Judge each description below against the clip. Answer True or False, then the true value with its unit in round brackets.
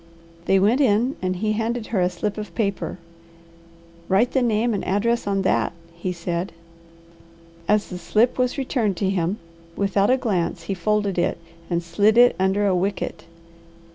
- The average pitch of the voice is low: False (200 Hz)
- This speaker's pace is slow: False (170 wpm)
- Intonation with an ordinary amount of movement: True (3.4 semitones)